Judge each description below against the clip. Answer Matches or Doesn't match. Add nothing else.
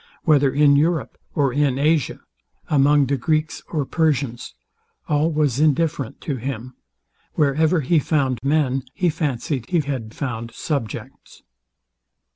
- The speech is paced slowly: Matches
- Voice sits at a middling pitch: Matches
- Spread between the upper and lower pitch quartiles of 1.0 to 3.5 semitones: Matches